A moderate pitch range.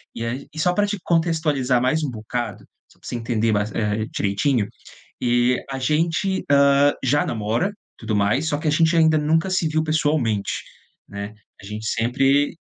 No: wide, 5.7 semitones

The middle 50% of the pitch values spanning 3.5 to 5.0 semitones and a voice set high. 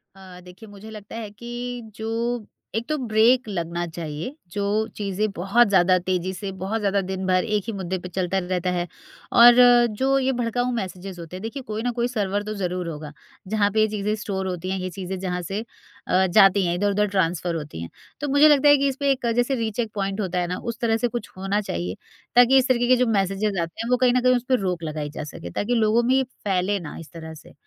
Yes: average, 4.5 semitones; high, 200 Hz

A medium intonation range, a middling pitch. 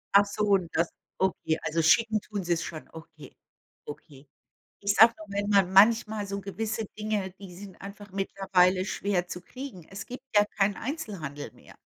No: average, 3.0 semitones; high, 195 Hz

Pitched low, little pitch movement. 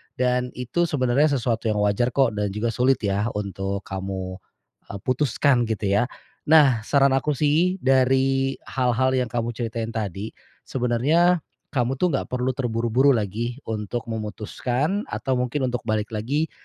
No: low, 125 Hz; average, 3.5 semitones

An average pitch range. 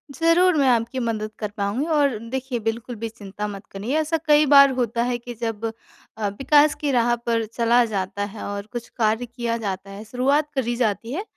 Yes: average, 3.6 semitones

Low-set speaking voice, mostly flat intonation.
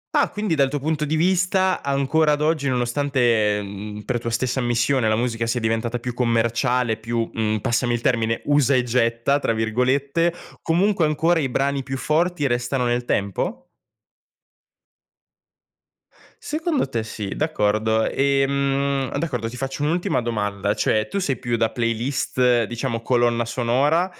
No: low, 125 Hz; average, 3.9 semitones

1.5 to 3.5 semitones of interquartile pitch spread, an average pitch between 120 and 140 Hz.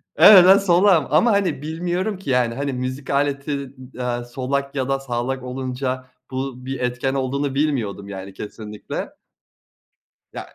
Yes: average, 2.7 semitones; low, 135 Hz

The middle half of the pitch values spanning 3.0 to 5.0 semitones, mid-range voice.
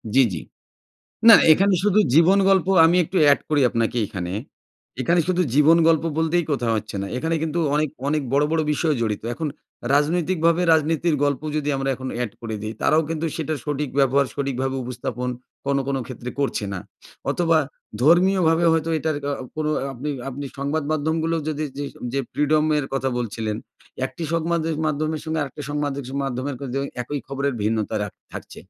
Yes: average, 3.5 semitones; medium, 150 Hz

